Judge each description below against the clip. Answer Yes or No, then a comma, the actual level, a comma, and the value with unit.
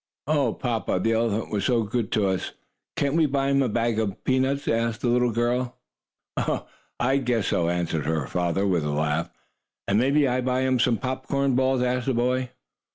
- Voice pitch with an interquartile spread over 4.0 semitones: Yes, average, 4.4 semitones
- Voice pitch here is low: Yes, low, 120 Hz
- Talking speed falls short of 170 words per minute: No, average, 190 wpm